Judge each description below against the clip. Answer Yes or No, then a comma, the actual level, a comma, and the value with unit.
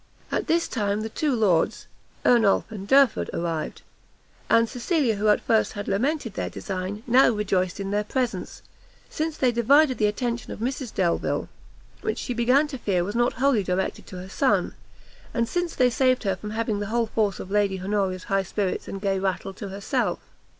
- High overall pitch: Yes, high, 215 Hz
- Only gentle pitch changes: No, average, 4.2 semitones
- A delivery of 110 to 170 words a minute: No, average, 185 wpm